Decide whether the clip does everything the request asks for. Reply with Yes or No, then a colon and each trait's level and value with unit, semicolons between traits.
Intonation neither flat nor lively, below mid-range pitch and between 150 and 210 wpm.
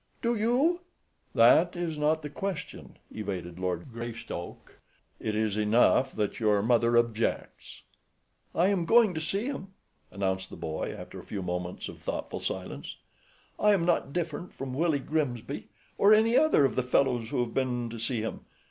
No: wide, 8.1 semitones; low, 130 Hz; average, 165 wpm